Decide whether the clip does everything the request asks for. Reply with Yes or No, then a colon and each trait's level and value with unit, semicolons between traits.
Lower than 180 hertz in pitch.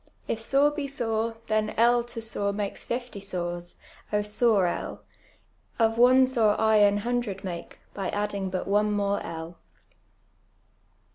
No: high, 210 Hz